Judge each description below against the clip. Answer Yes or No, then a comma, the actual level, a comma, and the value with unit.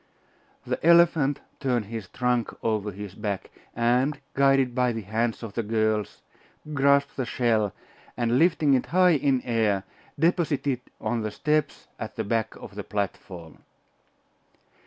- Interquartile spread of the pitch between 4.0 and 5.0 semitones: Yes, average, 4.4 semitones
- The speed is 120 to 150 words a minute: Yes, average, 145 wpm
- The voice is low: Yes, low, 120 Hz